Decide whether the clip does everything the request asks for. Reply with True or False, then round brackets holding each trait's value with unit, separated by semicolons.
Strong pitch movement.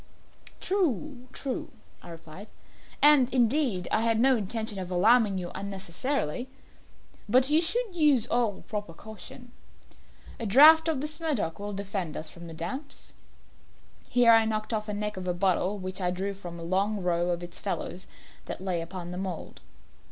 True (5.7 semitones)